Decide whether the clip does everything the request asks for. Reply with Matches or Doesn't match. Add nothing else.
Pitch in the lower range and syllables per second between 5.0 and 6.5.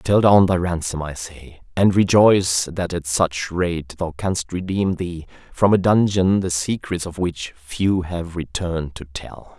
Doesn't match